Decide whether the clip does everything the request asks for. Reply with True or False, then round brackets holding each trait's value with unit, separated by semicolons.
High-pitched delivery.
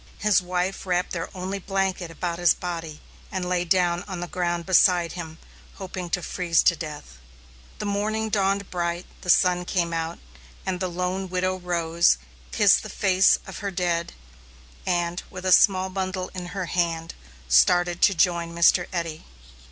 False (180 Hz)